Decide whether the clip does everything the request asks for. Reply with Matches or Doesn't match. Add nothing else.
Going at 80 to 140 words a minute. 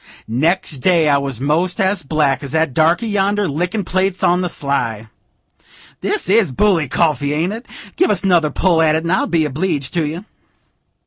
Doesn't match